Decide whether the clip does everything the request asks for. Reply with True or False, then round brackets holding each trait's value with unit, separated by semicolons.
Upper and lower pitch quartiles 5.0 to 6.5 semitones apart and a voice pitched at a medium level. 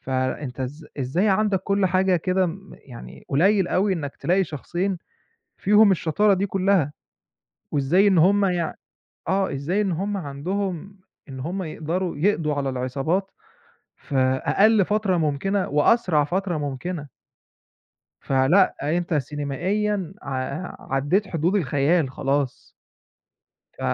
True (5.3 semitones; 175 Hz)